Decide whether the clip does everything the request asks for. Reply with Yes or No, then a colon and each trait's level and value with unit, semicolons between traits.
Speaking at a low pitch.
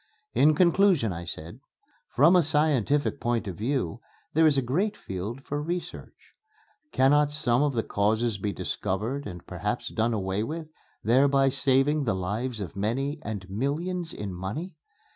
Yes: low, 130 Hz